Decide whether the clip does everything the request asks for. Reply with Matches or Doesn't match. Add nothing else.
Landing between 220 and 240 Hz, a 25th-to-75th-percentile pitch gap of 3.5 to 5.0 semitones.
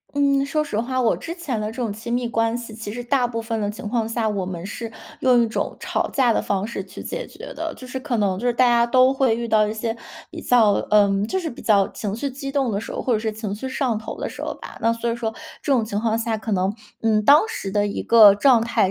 Doesn't match